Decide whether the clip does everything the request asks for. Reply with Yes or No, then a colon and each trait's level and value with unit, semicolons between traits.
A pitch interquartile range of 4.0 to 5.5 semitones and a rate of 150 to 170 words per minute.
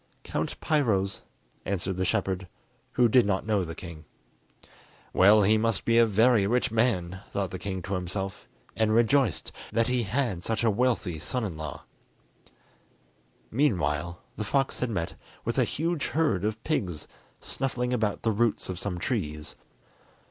Yes: average, 4.4 semitones; average, 155 wpm